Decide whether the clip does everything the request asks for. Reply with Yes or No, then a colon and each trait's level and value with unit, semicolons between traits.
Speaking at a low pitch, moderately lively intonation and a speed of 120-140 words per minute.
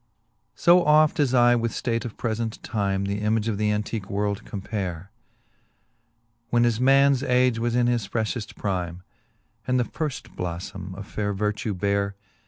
No: low, 110 Hz; average, 3.4 semitones; average, 165 wpm